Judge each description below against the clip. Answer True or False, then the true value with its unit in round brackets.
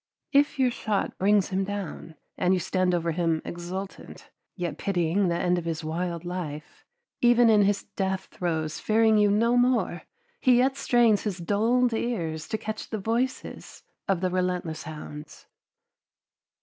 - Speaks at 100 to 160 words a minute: True (155 wpm)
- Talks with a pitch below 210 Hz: True (190 Hz)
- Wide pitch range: False (4.4 semitones)